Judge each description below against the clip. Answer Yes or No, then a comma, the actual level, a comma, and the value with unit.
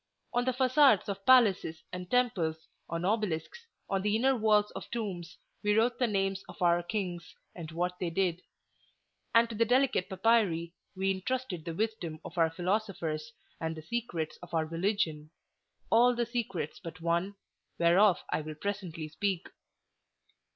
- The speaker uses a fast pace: No, average, 155 wpm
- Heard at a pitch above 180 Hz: Yes, high, 190 Hz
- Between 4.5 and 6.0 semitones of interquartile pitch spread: Yes, average, 4.9 semitones